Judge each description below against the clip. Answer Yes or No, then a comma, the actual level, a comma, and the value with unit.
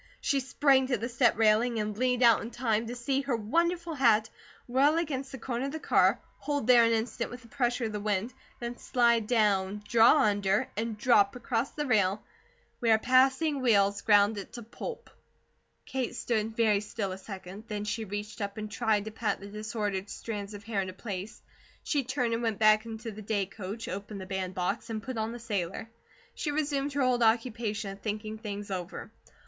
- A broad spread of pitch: No, average, 3.2 semitones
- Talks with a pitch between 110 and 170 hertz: No, high, 225 Hz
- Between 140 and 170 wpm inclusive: No, average, 195 wpm